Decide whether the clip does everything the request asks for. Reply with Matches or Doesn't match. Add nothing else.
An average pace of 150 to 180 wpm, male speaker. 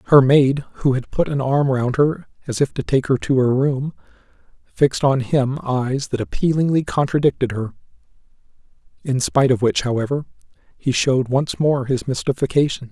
Matches